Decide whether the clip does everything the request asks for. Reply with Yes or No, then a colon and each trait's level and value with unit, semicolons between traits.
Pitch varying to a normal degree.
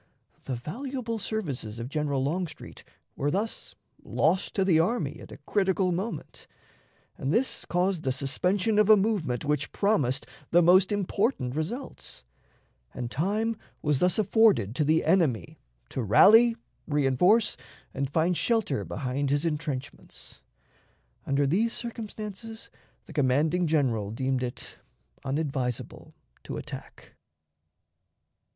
No: wide, 7.3 semitones